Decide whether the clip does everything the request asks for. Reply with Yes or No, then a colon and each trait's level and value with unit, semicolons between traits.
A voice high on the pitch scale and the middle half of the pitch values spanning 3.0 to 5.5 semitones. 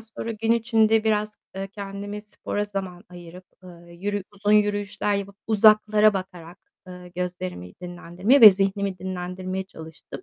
No: high, 195 Hz; narrow, 2.6 semitones